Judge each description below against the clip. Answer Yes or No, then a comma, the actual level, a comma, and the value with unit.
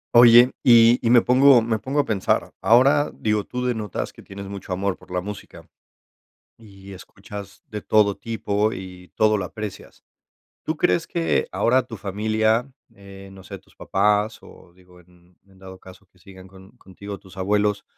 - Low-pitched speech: Yes, low, 105 Hz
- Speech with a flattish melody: No, average, 3.2 semitones